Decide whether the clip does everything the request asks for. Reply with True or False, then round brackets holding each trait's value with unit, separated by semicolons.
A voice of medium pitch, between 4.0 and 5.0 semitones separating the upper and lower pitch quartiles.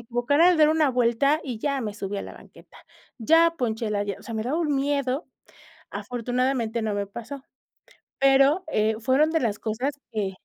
False (250 Hz; 4.6 semitones)